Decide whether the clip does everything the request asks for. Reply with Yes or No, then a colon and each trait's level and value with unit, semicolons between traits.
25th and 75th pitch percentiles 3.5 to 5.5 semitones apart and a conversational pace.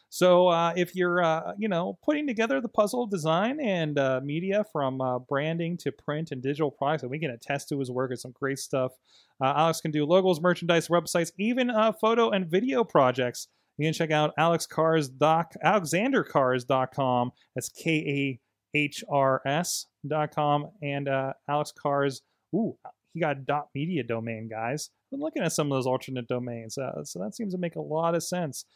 Yes: average, 4.7 semitones; average, 180 wpm